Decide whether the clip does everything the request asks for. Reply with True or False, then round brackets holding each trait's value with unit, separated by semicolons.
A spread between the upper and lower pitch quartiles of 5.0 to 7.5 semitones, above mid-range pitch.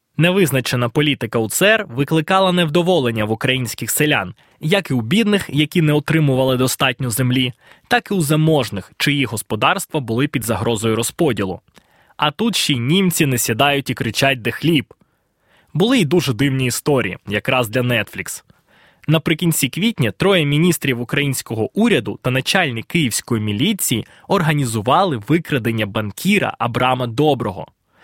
False (5.5 semitones; 140 Hz)